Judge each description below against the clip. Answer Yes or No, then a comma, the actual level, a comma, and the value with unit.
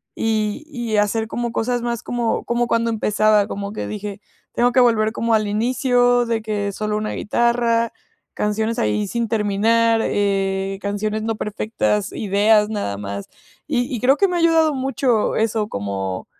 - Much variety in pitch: No, narrow, 2.4 semitones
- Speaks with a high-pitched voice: Yes, high, 220 Hz